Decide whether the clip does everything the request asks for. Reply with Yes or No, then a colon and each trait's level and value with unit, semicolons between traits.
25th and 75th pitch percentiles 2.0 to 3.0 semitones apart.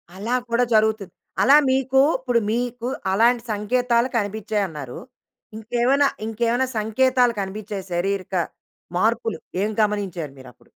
No: average, 3.5 semitones